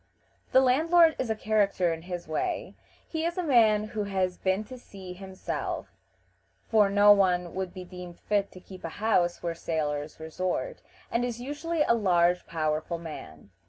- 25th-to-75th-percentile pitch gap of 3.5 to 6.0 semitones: Yes, average, 4.5 semitones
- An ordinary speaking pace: Yes, average, 175 wpm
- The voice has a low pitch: No, high, 190 Hz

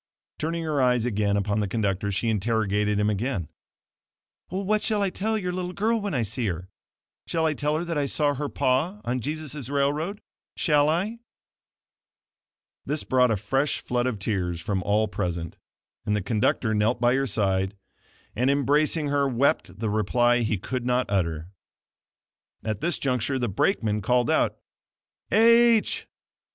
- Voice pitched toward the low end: Yes, low, 125 Hz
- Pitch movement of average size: No, wide, 6.5 semitones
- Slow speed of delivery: No, average, 160 wpm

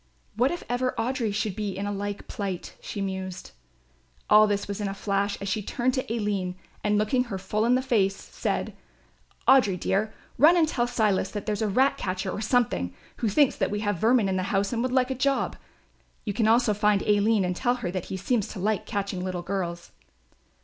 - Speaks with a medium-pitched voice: No, high, 210 Hz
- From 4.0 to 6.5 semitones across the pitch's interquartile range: No, average, 3.6 semitones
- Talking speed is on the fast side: Yes, fast, 210 wpm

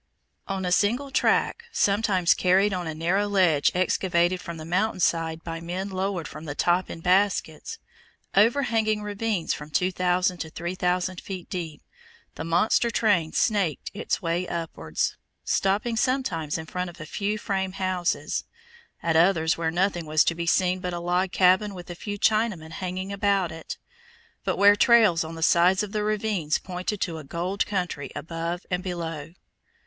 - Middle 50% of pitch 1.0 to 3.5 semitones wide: Yes, average, 3.2 semitones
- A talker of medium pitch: Yes, medium, 180 Hz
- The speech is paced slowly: No, average, 165 wpm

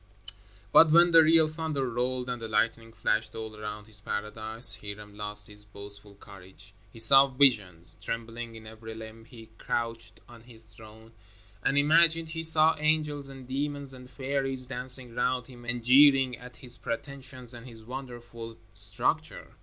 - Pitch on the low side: Yes, low, 120 Hz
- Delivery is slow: No, average, 160 wpm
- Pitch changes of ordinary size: Yes, average, 3.6 semitones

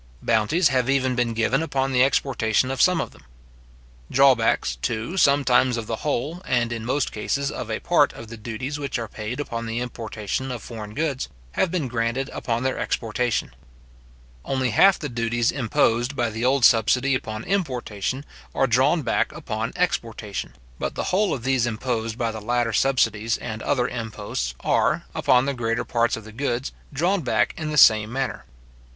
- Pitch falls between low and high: No, low, 125 Hz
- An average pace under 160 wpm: No, average, 180 wpm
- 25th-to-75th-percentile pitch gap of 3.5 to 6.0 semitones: No, average, 3.1 semitones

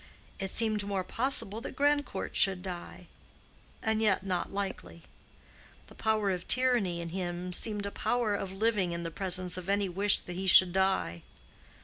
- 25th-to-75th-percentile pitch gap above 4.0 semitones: No, average, 3.0 semitones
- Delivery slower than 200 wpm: Yes, average, 160 wpm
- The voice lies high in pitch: Yes, high, 195 Hz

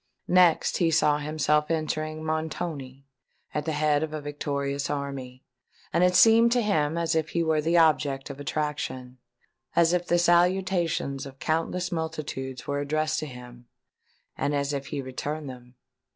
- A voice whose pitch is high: No, medium, 150 Hz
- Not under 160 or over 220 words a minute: No, average, 150 wpm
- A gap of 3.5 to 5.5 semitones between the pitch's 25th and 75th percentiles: No, average, 2.8 semitones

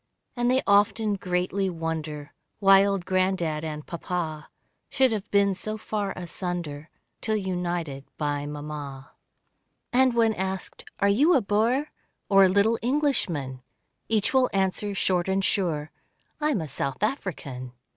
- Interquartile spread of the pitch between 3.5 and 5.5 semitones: Yes, average, 5.2 semitones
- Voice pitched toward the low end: No, high, 190 Hz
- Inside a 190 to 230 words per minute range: No, average, 140 wpm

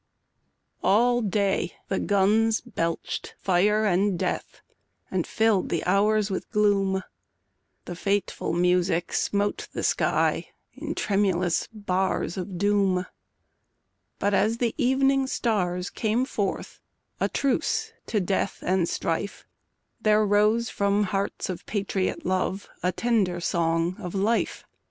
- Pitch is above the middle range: Yes, high, 200 Hz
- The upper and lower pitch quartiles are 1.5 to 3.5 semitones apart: Yes, average, 2.8 semitones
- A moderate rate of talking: No, slow, 120 wpm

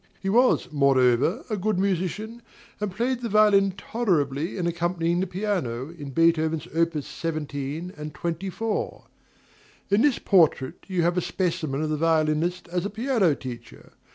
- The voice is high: No, medium, 170 Hz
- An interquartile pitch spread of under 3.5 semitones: No, average, 4.4 semitones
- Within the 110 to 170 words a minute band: Yes, average, 150 wpm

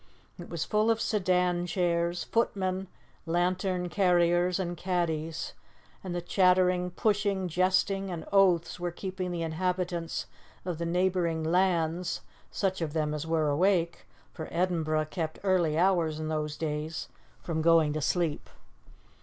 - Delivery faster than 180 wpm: No, slow, 135 wpm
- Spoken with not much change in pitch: Yes, narrow, 2.2 semitones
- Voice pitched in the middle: Yes, medium, 175 Hz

